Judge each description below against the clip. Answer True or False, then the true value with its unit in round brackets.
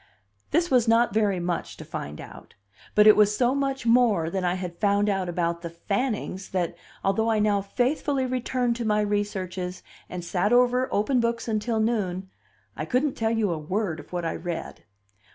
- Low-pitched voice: False (210 Hz)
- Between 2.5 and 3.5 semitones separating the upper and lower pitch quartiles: False (4.7 semitones)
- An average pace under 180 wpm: False (190 wpm)